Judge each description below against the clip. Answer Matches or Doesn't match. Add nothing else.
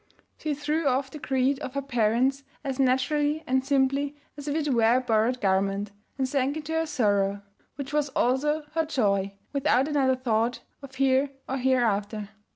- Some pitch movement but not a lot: Matches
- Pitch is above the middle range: Matches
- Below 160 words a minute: Doesn't match